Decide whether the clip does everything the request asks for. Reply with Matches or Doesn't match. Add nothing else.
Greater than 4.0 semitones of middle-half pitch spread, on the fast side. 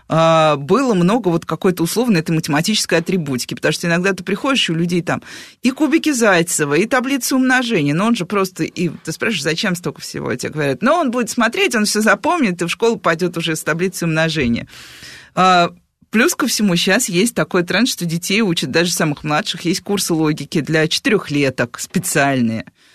Matches